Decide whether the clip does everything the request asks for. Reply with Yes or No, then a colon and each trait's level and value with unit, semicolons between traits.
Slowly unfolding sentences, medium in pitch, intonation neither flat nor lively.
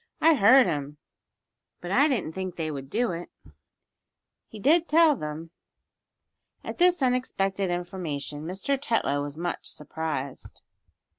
No: slow, 130 wpm; medium, 180 Hz; wide, 8.6 semitones